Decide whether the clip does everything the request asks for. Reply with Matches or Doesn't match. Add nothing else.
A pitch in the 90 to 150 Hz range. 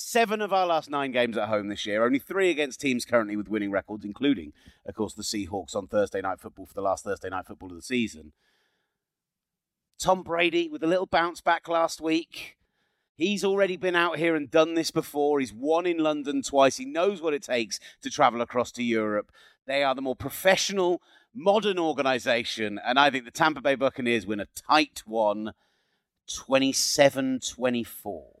Matches